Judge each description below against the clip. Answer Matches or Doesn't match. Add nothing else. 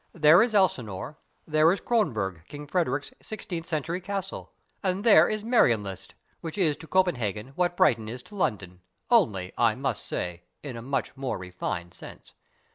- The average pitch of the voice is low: Doesn't match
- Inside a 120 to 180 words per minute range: Matches